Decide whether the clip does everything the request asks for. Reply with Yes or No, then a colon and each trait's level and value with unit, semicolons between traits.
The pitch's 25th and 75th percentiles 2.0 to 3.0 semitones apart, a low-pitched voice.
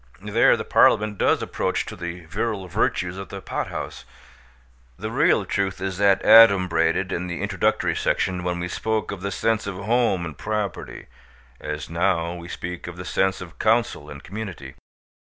Yes: narrow, 2.6 semitones; very low, 95 Hz